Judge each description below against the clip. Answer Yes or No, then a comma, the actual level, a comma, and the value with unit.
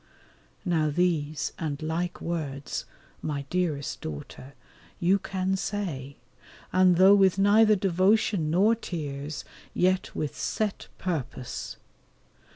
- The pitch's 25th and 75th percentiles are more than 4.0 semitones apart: Yes, average, 4.5 semitones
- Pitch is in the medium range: Yes, medium, 175 Hz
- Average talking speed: No, slow, 105 wpm